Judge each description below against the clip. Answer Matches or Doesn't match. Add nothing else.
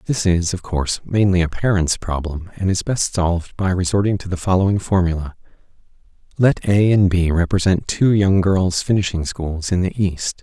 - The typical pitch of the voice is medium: Doesn't match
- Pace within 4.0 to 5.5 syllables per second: Matches